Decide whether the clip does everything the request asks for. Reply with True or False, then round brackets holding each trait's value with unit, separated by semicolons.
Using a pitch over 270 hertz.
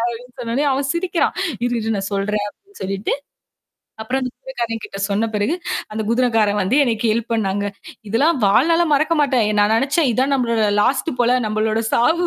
False (235 Hz)